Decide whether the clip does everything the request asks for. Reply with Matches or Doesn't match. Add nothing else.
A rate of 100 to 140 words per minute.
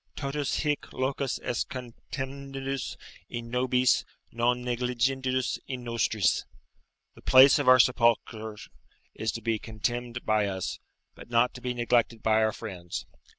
Matches